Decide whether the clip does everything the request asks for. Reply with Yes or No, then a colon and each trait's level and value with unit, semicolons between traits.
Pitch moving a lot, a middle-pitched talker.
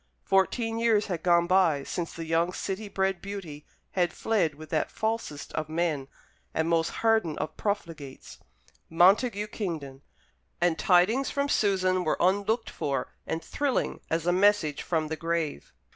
No: average, 4.1 semitones; medium, 175 Hz